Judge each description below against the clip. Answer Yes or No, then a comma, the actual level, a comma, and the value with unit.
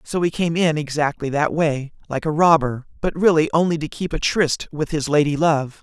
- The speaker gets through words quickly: Yes, fast, 215 wpm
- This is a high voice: No, medium, 155 Hz